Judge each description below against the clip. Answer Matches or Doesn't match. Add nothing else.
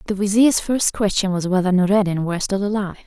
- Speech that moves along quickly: Doesn't match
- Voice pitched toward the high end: Matches